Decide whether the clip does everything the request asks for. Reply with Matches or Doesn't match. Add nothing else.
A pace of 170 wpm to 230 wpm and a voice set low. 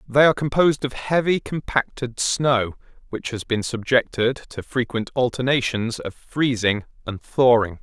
Doesn't match